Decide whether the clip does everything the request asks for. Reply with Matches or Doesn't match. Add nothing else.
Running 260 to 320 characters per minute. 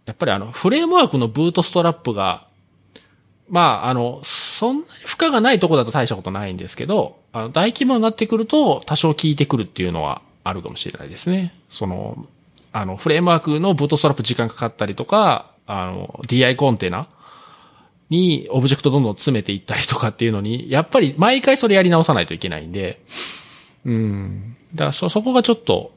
Doesn't match